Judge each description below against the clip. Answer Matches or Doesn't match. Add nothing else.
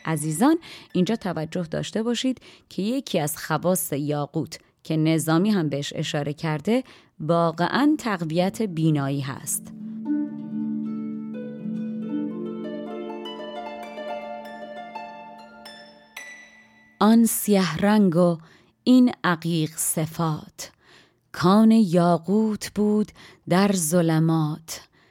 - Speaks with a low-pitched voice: Doesn't match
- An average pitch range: Doesn't match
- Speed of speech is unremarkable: Doesn't match